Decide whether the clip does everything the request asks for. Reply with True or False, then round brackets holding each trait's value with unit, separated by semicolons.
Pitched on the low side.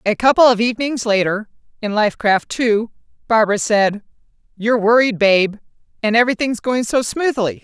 False (225 Hz)